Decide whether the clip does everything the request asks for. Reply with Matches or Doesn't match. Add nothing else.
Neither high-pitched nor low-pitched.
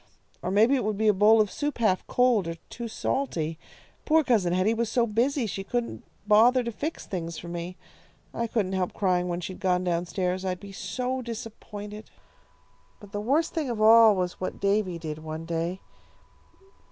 Doesn't match